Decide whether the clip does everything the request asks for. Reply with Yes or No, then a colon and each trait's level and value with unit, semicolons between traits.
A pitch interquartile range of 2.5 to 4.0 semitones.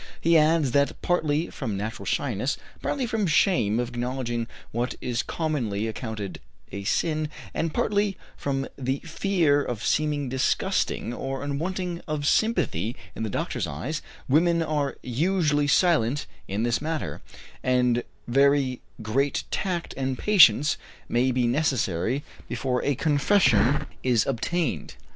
No: average, 4.8 semitones